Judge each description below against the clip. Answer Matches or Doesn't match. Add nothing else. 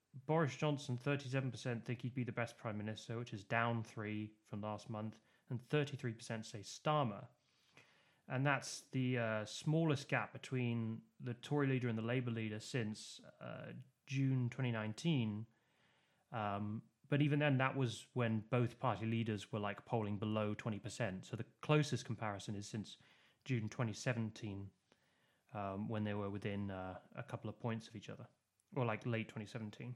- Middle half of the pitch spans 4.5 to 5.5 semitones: Doesn't match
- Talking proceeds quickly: Doesn't match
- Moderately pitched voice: Doesn't match